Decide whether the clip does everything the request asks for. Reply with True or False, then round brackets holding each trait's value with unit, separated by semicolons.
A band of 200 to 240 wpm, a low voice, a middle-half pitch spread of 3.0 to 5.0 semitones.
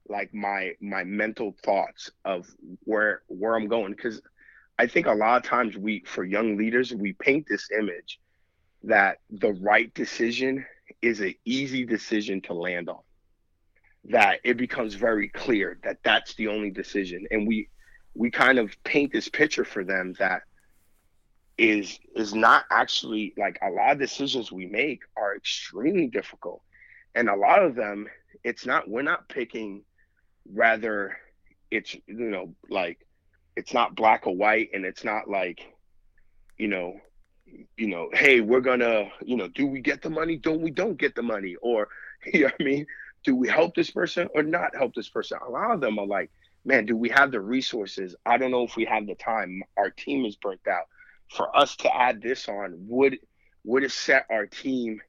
False (185 wpm; 115 Hz; 4.1 semitones)